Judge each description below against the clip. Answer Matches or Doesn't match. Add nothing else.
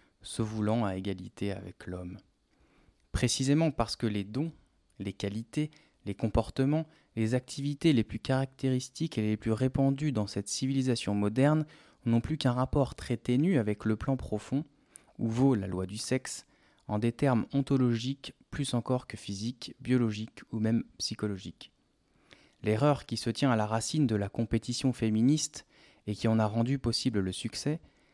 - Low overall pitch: Matches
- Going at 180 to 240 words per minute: Doesn't match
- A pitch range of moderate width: Matches